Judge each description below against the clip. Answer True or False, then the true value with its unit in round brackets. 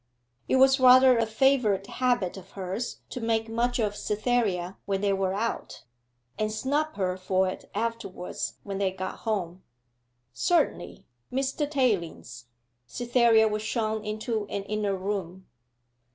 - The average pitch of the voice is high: True (215 Hz)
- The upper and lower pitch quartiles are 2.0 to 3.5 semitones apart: False (4.1 semitones)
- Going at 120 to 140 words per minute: True (135 wpm)